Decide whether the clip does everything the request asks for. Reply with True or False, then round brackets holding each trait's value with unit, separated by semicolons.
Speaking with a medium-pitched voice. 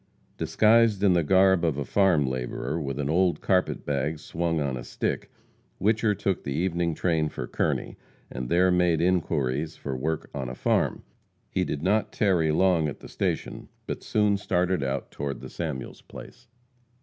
False (80 Hz)